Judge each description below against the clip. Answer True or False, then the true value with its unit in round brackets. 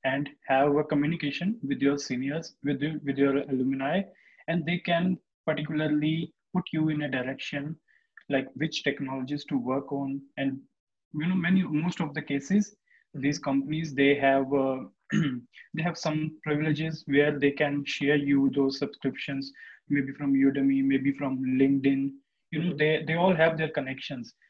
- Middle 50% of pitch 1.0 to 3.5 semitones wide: True (2.6 semitones)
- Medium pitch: True (145 Hz)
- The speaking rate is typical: True (160 wpm)